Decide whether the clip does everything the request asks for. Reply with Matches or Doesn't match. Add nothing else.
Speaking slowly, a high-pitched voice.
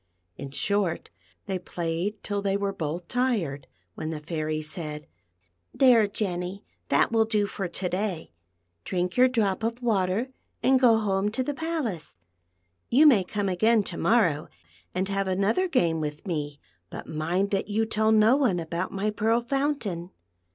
Doesn't match